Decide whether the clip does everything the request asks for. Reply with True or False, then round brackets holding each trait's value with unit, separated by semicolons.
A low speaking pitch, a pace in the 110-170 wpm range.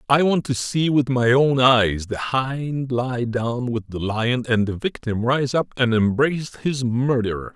False (125 Hz; 190 wpm)